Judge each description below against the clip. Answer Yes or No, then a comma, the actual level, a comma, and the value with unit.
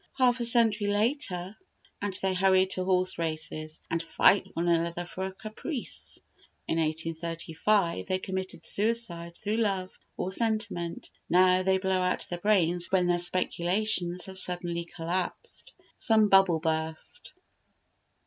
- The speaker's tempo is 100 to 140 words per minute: Yes, slow, 135 wpm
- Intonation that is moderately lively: Yes, average, 3.1 semitones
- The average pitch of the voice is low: No, medium, 185 Hz